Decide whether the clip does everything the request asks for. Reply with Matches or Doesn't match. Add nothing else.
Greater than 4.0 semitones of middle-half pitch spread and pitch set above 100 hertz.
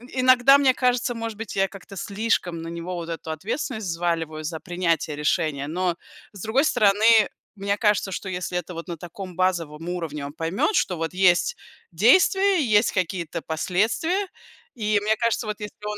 Matches